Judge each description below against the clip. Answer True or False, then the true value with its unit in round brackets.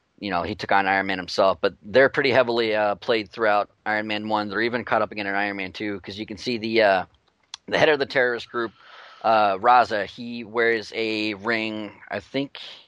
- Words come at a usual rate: False (220 wpm)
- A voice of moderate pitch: False (110 Hz)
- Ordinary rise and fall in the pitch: False (2.2 semitones)